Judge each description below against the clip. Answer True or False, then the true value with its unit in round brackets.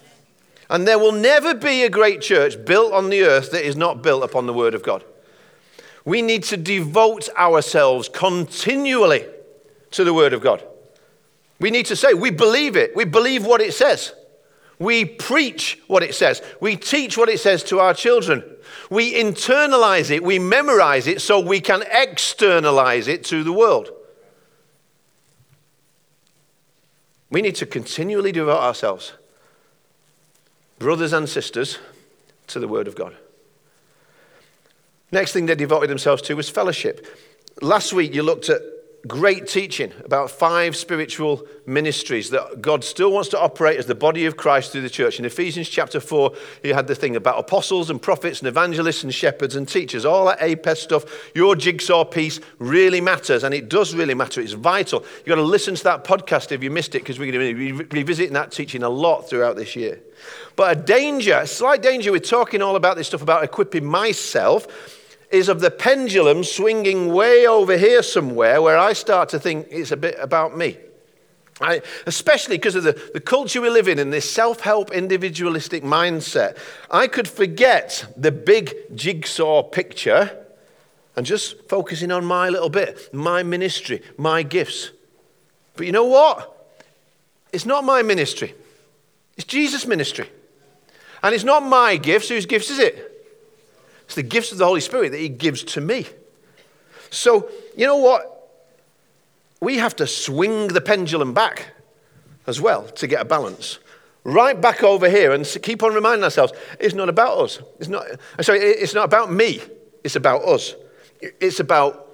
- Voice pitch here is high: True (205 Hz)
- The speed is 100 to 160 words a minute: False (170 wpm)